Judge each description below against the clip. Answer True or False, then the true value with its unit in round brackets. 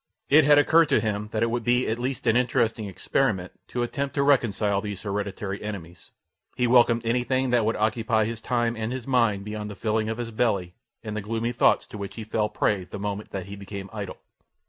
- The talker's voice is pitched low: True (110 Hz)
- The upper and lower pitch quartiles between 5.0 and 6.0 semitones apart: False (2.8 semitones)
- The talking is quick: True (215 wpm)